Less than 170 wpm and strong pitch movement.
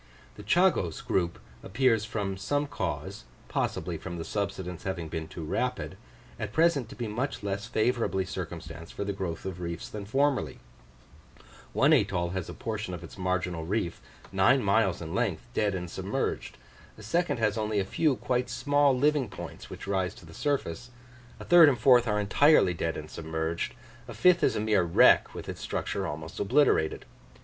No: average, 175 wpm; wide, 5.9 semitones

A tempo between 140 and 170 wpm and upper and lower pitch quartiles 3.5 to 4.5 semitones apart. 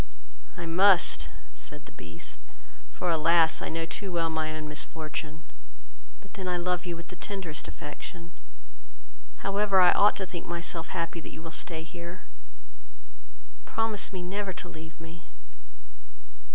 No: average, 150 wpm; narrow, 2.5 semitones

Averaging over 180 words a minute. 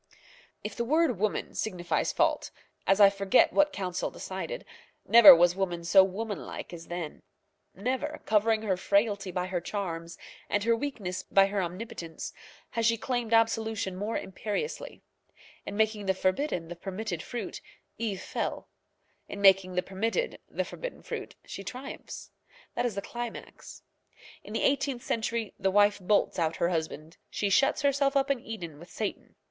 No: average, 160 wpm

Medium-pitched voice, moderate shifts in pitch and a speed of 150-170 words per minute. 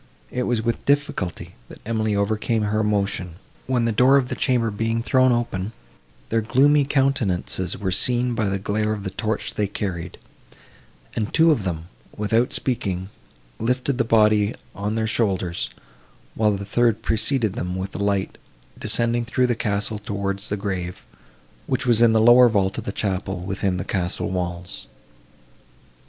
No: low, 110 Hz; average, 3.3 semitones; average, 165 wpm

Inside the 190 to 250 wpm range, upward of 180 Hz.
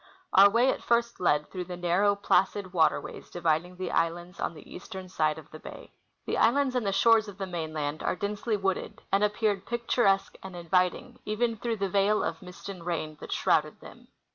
Yes: average, 200 wpm; high, 190 Hz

